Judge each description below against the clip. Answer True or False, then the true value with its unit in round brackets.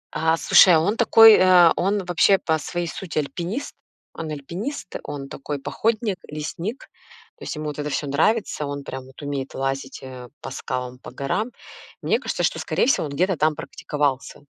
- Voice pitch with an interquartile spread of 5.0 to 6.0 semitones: True (5.3 semitones)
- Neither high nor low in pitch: True (155 Hz)